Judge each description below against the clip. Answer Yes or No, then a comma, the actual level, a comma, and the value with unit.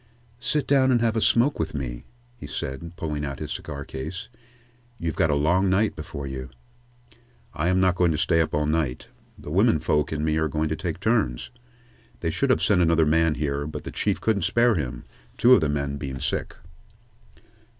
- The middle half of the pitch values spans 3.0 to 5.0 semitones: Yes, average, 4.2 semitones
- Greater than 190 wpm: Yes, average, 200 wpm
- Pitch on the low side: Yes, very low, 80 Hz